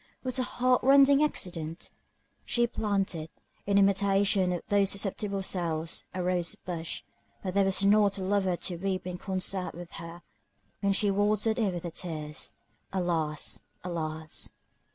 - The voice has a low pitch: No, high, 190 Hz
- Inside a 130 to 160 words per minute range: Yes, average, 150 wpm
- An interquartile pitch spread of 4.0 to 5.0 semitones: No, average, 2.8 semitones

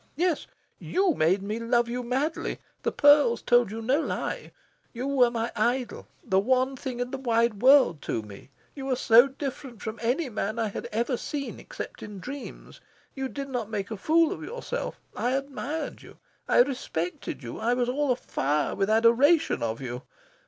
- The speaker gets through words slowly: No, average, 180 wpm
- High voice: Yes, high, 245 Hz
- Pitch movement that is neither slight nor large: Yes, average, 3.9 semitones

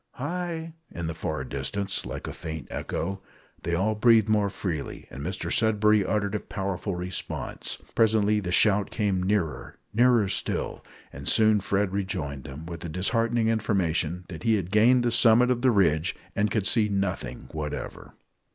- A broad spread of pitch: No, average, 4.2 semitones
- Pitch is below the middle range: Yes, low, 100 Hz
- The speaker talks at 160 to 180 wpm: Yes, average, 165 wpm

